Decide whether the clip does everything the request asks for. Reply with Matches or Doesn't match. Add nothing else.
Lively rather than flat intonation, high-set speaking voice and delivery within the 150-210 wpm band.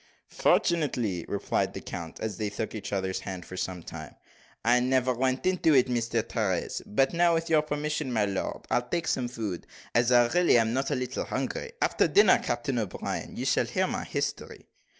Doesn't match